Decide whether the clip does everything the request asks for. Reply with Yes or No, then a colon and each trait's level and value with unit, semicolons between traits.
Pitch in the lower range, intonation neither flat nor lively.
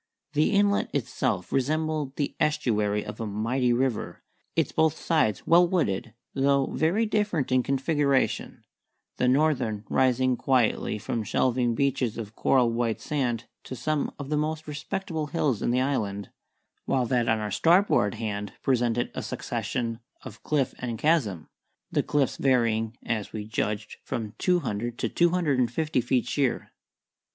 Yes: low, 130 Hz; average, 4.8 semitones